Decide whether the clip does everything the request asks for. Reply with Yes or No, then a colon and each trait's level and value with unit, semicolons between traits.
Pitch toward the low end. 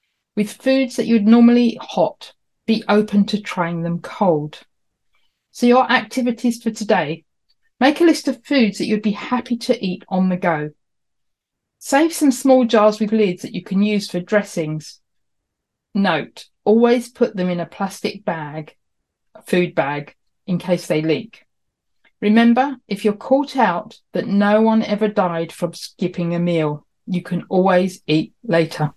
No: high, 205 Hz